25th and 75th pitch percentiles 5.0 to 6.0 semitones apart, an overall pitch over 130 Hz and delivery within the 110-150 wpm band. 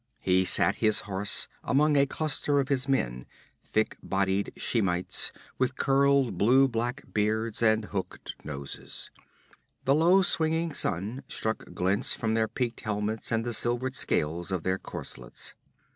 No: wide, 5.6 semitones; low, 115 Hz; average, 145 wpm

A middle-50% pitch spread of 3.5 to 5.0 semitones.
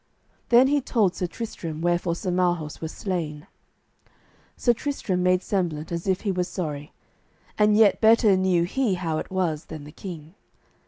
Yes: average, 3.8 semitones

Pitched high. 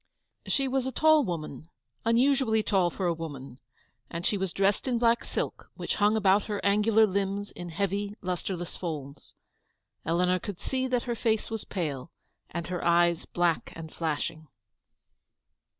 Yes: high, 195 Hz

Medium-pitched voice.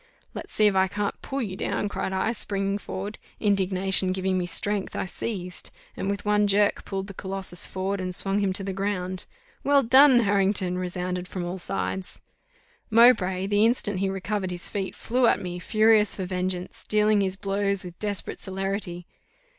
No: high, 195 Hz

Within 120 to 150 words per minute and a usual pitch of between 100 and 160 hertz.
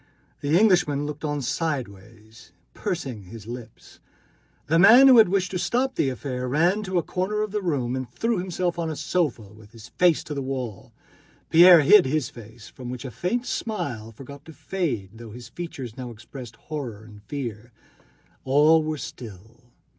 No: average, 180 wpm; medium, 140 Hz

